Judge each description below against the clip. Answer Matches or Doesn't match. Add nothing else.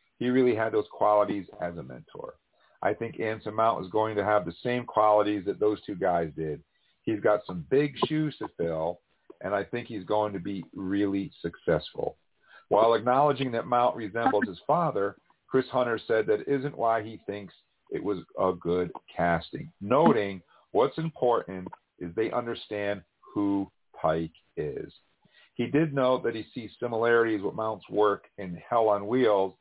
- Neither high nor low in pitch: Doesn't match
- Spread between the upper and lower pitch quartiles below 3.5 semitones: Doesn't match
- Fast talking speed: Doesn't match